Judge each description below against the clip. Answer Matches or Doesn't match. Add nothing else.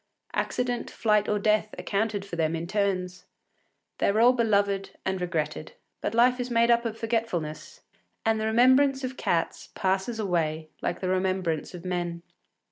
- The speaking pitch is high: Matches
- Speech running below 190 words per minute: Matches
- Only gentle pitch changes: Doesn't match